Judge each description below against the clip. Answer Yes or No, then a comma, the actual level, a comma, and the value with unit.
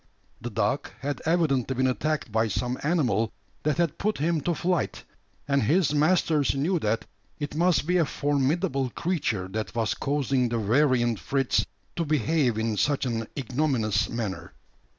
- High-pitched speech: No, medium, 140 Hz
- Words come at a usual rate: Yes, average, 155 wpm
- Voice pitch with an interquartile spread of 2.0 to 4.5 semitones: No, average, 5.0 semitones